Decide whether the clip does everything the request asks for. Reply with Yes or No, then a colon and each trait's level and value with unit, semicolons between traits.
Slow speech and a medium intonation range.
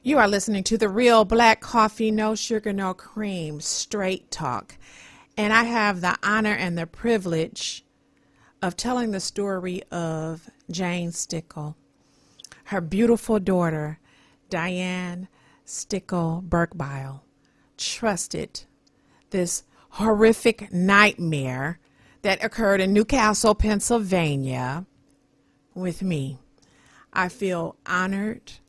Yes: slow, 100 wpm; average, 4.5 semitones